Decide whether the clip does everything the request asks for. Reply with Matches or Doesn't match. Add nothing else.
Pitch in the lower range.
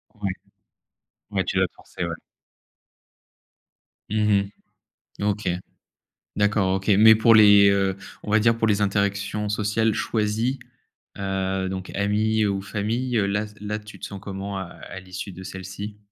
Matches